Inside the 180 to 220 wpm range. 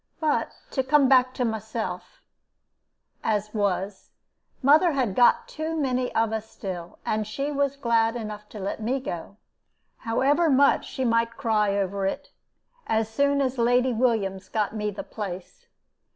No: average, 150 wpm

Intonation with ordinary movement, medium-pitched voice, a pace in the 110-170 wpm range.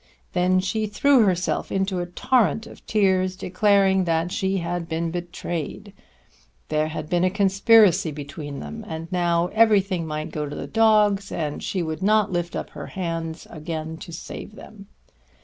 Yes: average, 3.4 semitones; medium, 180 Hz; average, 165 wpm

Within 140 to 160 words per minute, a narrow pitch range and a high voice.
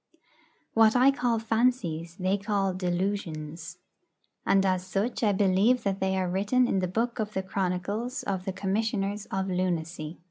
No: average, 155 wpm; average, 3.1 semitones; high, 195 Hz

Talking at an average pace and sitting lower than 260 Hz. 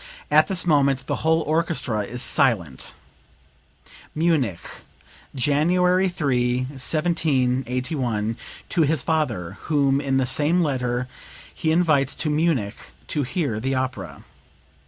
No: slow, 115 wpm; medium, 140 Hz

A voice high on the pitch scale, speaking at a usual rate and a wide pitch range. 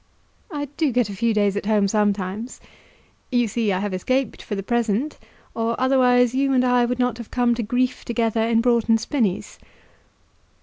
No: high, 235 Hz; average, 180 wpm; average, 3.0 semitones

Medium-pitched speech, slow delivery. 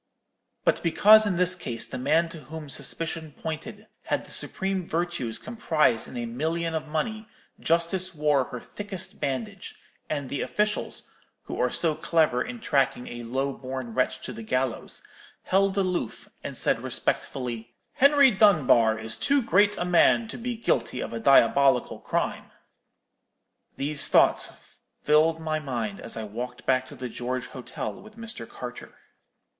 No: medium, 150 Hz; average, 155 wpm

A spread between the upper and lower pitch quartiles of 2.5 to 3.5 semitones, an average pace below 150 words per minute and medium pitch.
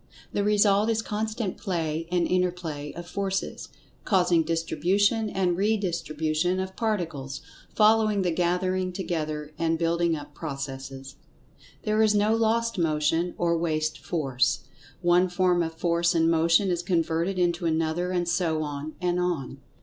Yes: average, 2.9 semitones; average, 140 wpm; medium, 175 Hz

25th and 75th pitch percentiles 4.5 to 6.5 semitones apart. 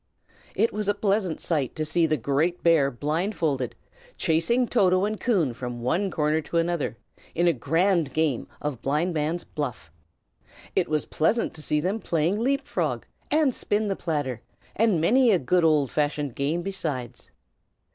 Yes: average, 4.9 semitones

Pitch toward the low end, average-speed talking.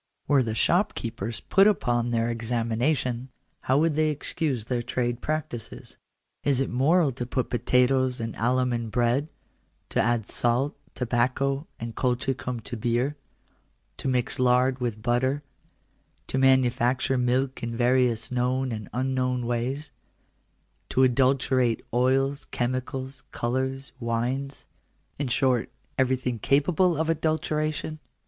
No: low, 125 Hz; slow, 125 wpm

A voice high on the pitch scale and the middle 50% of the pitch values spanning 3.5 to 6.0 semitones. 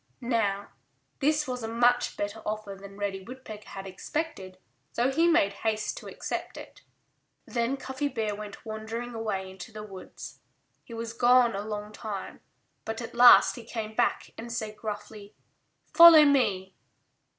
No: high, 220 Hz; average, 3.1 semitones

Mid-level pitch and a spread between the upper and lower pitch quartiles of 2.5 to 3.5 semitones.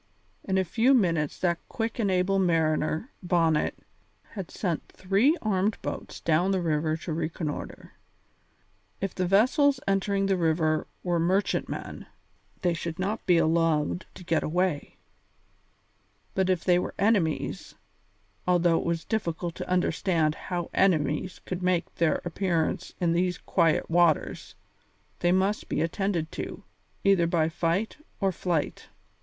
Yes: medium, 175 Hz; average, 2.8 semitones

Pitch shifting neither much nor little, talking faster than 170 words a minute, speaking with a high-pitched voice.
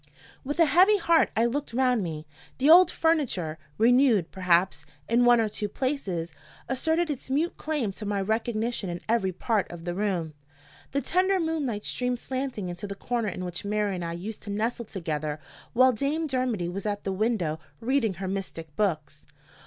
No: wide, 6.1 semitones; average, 180 wpm; high, 220 Hz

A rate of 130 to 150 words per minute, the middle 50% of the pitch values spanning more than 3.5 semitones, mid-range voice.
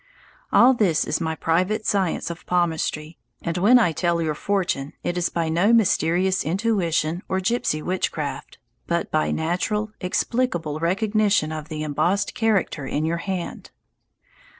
Yes: average, 145 wpm; average, 4.0 semitones; medium, 175 Hz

